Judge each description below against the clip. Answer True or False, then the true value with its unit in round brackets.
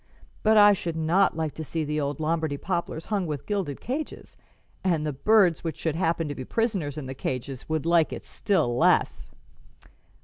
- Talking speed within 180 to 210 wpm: True (190 wpm)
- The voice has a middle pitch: True (160 Hz)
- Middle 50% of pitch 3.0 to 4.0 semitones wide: False (4.4 semitones)